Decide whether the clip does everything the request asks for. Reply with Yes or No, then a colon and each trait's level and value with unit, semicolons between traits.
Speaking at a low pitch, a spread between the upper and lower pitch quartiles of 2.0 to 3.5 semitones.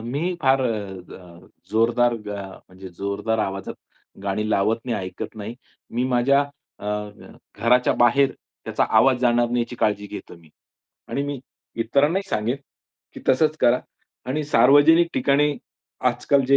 No: low, 120 Hz; average, 4.6 semitones